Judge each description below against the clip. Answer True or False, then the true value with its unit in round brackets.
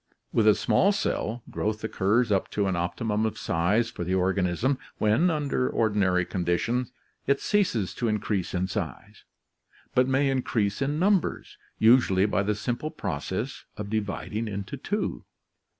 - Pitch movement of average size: True (4.7 semitones)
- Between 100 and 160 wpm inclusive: True (150 wpm)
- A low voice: True (110 Hz)